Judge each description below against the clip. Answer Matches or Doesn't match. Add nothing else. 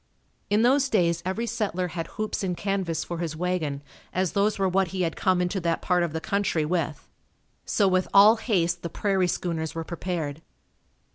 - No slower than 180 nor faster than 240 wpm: Matches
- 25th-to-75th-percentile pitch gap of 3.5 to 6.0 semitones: Doesn't match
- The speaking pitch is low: Doesn't match